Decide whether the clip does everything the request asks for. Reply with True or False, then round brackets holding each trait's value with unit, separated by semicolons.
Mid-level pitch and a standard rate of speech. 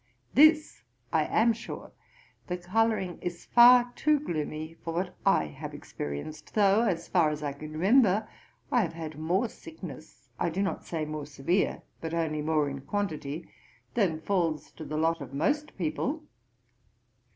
True (170 Hz; 160 wpm)